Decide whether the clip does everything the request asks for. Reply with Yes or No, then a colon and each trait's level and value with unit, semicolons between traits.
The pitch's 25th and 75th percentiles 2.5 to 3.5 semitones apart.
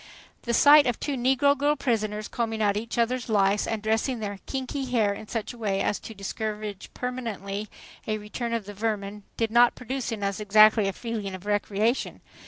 Yes: average, 2.8 semitones